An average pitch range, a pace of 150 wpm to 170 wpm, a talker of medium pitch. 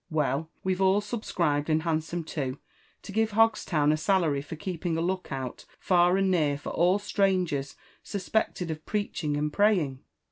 Yes: average, 4.3 semitones; average, 165 wpm; medium, 170 Hz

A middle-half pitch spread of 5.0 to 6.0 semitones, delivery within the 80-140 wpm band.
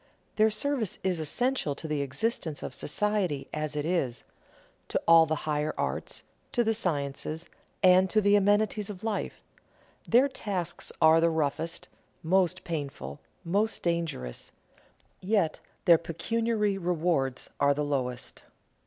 Yes: wide, 5.5 semitones; slow, 135 wpm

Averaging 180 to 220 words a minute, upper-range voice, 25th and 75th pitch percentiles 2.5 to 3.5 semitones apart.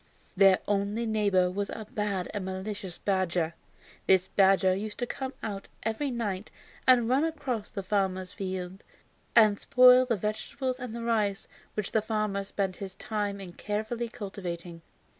No: average, 160 wpm; high, 205 Hz; average, 3.0 semitones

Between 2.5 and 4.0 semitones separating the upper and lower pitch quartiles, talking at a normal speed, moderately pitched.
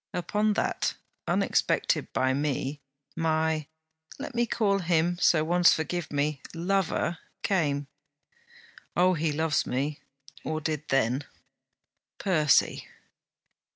No: average, 3.3 semitones; slow, 105 wpm; medium, 160 Hz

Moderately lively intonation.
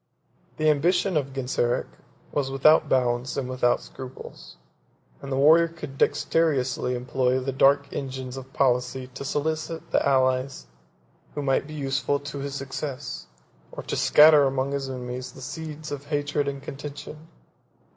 No: narrow, 2.1 semitones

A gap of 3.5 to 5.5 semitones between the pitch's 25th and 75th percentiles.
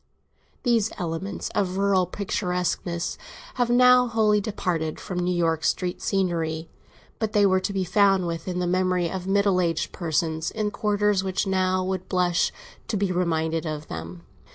No: average, 2.9 semitones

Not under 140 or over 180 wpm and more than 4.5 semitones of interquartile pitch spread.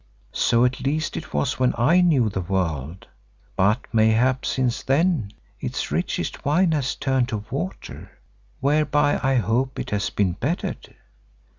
Yes: average, 145 wpm; average, 5.2 semitones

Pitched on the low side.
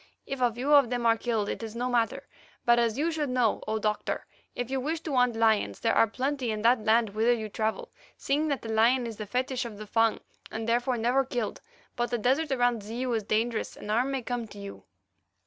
No: high, 235 Hz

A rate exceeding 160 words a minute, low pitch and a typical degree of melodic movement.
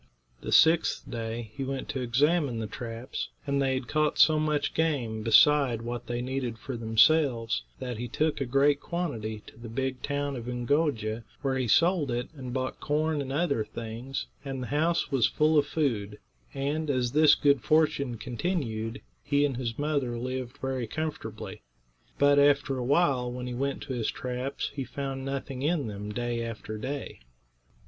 Yes: average, 175 wpm; low, 130 Hz; average, 3.4 semitones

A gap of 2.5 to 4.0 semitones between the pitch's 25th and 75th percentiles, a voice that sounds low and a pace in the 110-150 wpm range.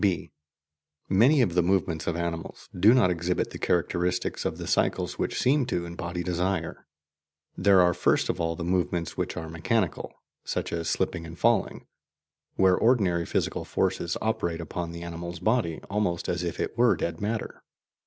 No: average, 3.1 semitones; very low, 90 Hz; average, 170 wpm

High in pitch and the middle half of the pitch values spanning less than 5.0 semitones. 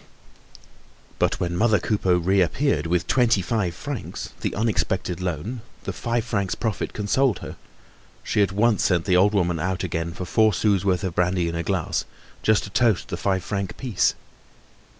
No: very low, 95 Hz; average, 3.5 semitones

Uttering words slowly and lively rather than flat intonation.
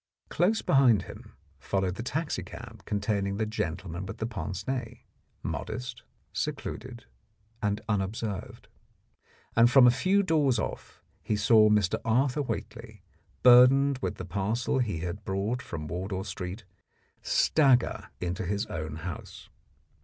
No: slow, 125 wpm; average, 4.7 semitones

